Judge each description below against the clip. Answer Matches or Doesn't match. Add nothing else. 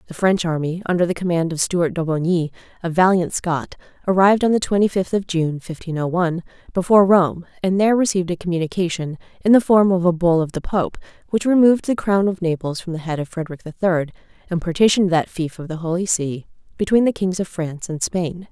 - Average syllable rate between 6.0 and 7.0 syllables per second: Matches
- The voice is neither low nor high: Matches